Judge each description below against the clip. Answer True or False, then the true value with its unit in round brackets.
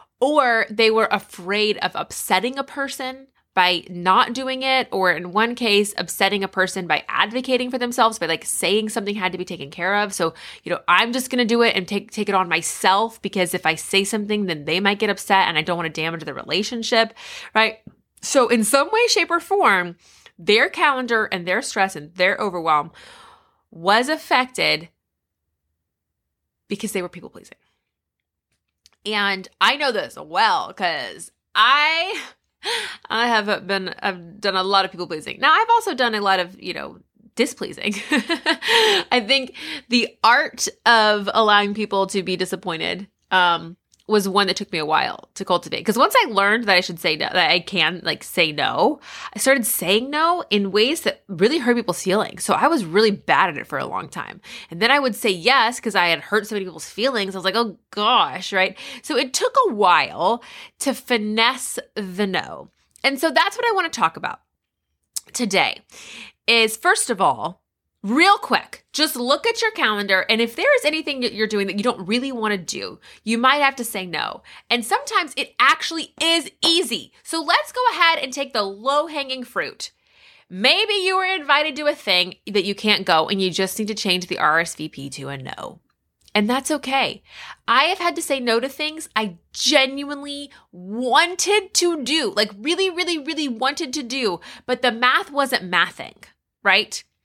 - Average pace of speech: True (190 wpm)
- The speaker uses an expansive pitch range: True (6.5 semitones)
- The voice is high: True (220 Hz)